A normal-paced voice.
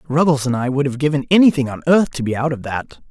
No: fast, 270 wpm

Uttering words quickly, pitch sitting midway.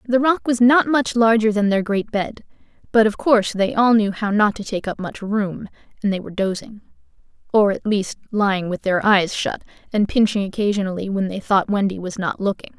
No: fast, 210 wpm; high, 210 Hz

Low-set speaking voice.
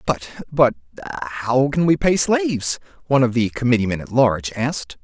Yes: low, 125 Hz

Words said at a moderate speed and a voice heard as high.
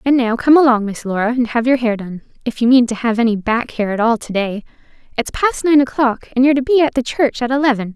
No: fast, 270 wpm; high, 245 Hz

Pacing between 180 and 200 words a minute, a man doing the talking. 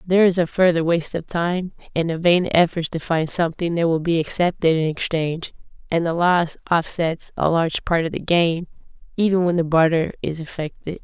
No: average, 195 wpm; female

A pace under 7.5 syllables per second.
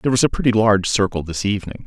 No: 7.7 syllables/s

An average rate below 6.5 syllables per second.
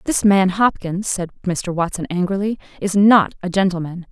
Yes: 4.9 syllables/s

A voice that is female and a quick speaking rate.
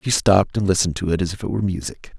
No: male; fast, 300 wpm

